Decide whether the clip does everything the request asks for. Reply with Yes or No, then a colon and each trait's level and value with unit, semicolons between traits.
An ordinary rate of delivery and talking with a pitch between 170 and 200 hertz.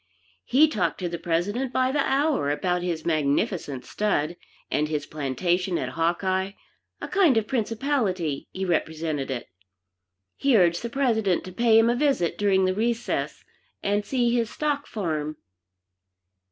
Yes: average, 150 wpm; high, 190 Hz